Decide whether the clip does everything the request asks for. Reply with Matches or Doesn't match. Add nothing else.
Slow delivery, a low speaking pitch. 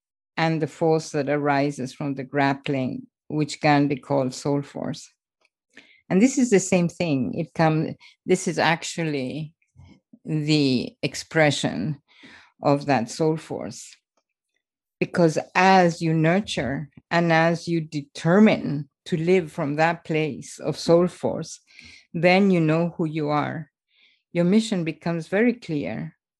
Doesn't match